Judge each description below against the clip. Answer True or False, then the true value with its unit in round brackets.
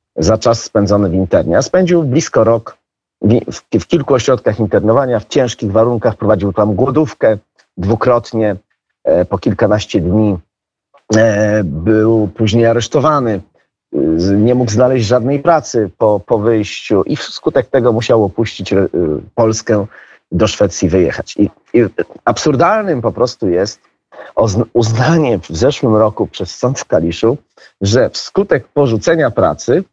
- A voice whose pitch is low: True (110 Hz)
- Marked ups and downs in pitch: False (2.7 semitones)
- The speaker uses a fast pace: False (135 wpm)